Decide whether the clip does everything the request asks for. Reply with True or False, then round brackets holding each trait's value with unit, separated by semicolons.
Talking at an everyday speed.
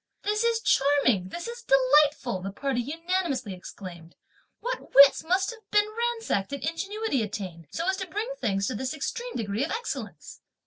True (170 wpm)